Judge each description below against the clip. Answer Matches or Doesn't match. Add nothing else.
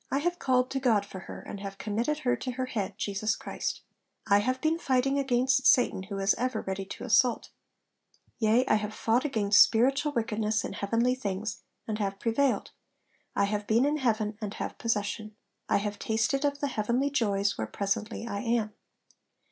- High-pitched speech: Matches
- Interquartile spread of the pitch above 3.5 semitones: Matches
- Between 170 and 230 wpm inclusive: Matches